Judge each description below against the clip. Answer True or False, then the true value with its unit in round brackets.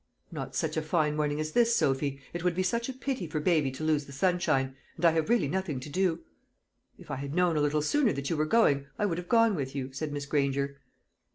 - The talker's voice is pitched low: False (155 Hz)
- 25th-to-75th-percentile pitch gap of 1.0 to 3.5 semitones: False (4.3 semitones)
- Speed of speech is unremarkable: False (250 wpm)